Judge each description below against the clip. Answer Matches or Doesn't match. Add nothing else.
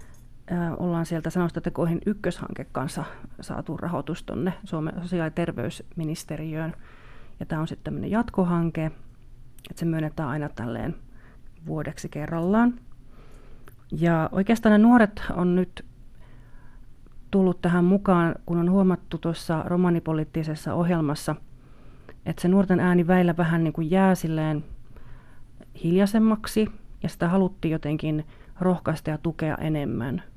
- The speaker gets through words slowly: Doesn't match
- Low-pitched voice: Doesn't match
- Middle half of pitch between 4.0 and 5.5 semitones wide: Doesn't match